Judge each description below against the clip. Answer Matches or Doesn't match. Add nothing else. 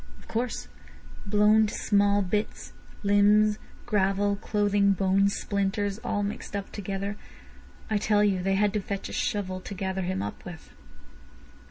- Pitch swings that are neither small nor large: Doesn't match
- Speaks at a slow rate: Doesn't match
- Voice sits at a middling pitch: Doesn't match